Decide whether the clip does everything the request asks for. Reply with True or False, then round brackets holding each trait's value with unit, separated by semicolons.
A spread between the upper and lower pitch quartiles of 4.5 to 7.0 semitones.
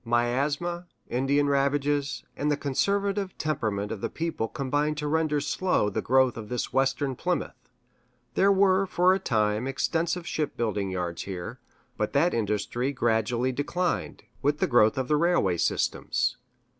True (5.4 semitones)